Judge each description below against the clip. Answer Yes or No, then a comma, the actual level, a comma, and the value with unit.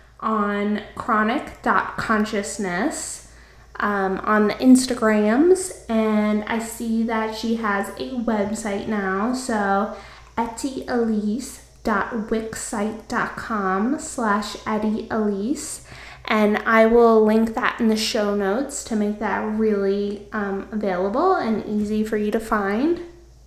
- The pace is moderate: No, slow, 100 wpm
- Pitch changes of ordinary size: No, narrow, 1.8 semitones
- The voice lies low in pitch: No, high, 220 Hz